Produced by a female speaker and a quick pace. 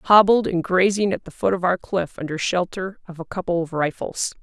Yes: female; fast, 215 wpm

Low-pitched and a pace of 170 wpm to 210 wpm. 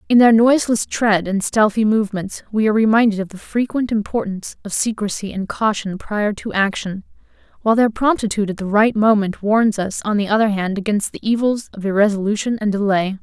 No: high, 210 Hz; average, 185 wpm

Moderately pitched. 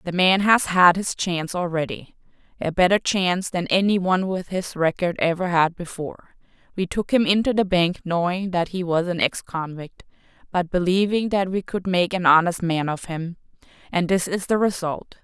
Yes: medium, 180 Hz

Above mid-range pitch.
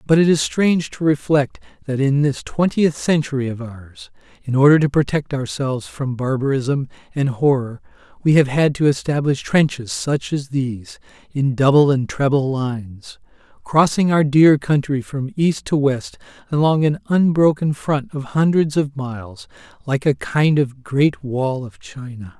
No: medium, 140 Hz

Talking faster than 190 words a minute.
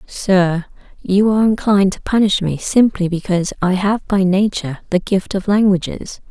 No: average, 160 wpm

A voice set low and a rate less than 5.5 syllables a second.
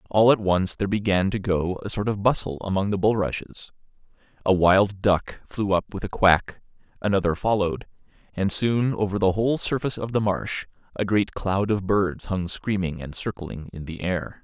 Yes: low, 100 Hz; 5.0 syllables/s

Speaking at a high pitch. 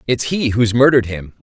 No: low, 115 Hz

